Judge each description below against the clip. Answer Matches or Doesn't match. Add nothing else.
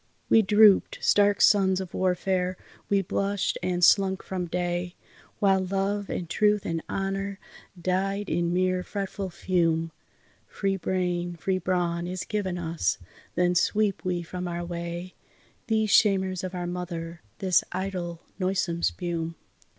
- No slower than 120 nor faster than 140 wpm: Matches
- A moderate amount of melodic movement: Doesn't match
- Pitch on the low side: Doesn't match